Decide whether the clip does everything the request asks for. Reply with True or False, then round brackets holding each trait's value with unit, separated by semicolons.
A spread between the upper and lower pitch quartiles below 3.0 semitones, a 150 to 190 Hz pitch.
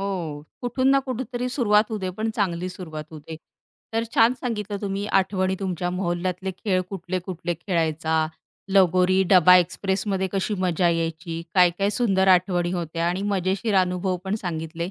True (2.5 semitones; 185 Hz)